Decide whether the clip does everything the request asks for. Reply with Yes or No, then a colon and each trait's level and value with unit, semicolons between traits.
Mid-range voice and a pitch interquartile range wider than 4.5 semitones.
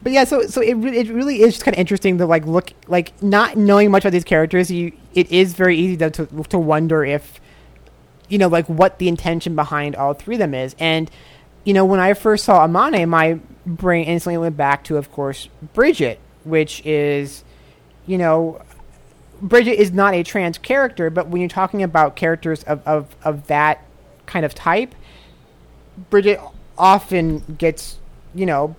No: medium, 170 Hz; average, 3.8 semitones